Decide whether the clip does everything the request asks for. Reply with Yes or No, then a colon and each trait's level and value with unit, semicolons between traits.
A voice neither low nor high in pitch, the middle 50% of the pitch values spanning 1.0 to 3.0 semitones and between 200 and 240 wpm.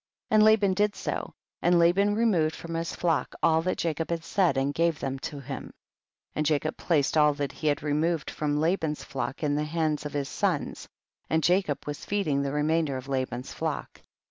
Yes: medium, 155 Hz; average, 2.7 semitones; fast, 205 wpm